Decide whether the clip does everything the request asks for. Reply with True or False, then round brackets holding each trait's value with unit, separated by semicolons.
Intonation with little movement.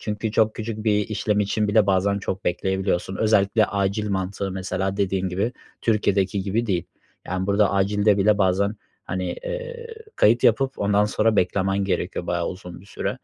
True (2.0 semitones)